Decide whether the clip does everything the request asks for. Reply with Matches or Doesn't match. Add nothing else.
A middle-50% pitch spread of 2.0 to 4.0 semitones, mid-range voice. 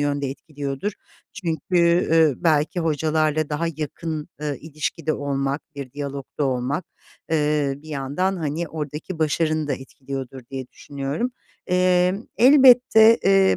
Matches